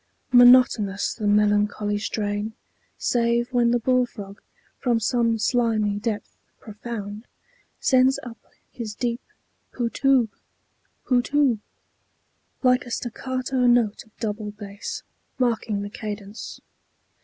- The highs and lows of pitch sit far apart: No, average, 2.9 semitones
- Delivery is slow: Yes, slow, 110 wpm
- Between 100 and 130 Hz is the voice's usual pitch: No, high, 230 Hz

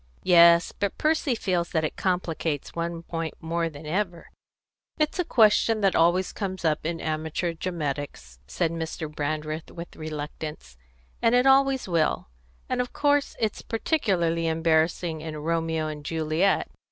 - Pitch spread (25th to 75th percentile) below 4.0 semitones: Yes, average, 3.5 semitones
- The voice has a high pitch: No, medium, 165 Hz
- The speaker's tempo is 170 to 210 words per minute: No, average, 150 wpm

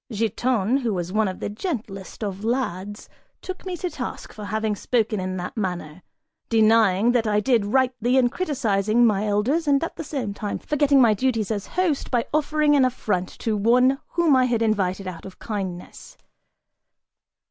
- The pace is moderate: Yes, average, 175 wpm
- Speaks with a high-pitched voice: Yes, high, 225 Hz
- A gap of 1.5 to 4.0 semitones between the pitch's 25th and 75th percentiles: No, average, 4.4 semitones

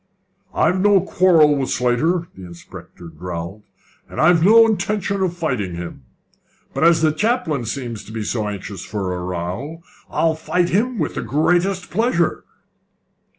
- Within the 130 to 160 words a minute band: Yes, average, 150 wpm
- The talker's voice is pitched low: No, medium, 155 Hz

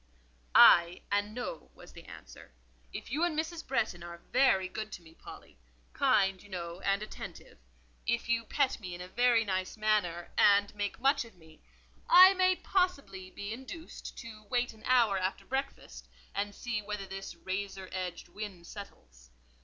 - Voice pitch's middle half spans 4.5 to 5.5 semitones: Yes, average, 4.9 semitones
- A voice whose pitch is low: No, high, 205 Hz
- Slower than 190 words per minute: Yes, average, 165 wpm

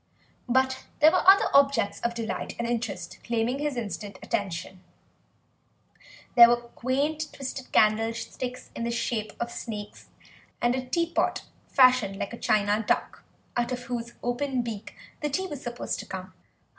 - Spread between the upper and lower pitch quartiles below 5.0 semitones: Yes, average, 2.9 semitones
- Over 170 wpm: No, average, 150 wpm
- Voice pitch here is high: Yes, high, 240 Hz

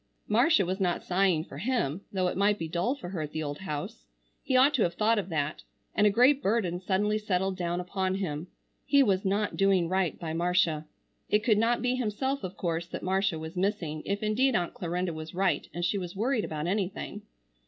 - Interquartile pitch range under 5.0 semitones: Yes, average, 3.6 semitones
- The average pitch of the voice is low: No, high, 190 Hz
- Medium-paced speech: No, fast, 215 wpm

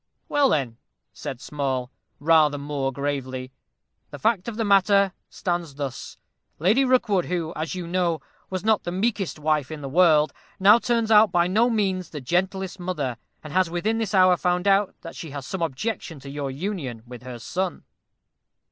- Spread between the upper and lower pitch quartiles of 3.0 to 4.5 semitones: No, wide, 5.4 semitones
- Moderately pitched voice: Yes, medium, 175 Hz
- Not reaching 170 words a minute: No, average, 175 wpm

